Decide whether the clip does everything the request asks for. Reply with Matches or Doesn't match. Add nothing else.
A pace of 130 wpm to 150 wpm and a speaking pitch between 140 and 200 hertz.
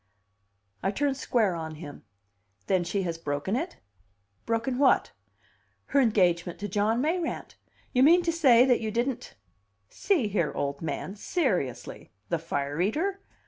Doesn't match